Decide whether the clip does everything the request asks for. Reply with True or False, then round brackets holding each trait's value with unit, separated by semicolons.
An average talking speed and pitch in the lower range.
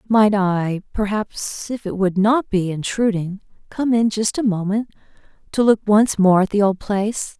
False (180 wpm; 205 Hz)